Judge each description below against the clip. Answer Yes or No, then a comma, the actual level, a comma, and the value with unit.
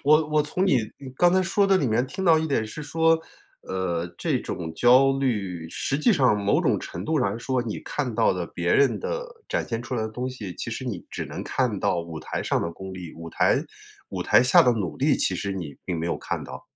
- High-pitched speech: No, low, 120 Hz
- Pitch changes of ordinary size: No, wide, 8.2 semitones